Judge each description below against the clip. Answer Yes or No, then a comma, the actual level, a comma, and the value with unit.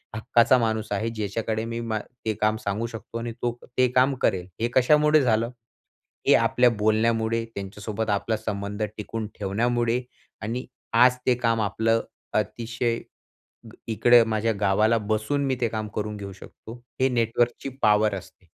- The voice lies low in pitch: Yes, low, 115 Hz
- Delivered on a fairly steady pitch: Yes, narrow, 1.9 semitones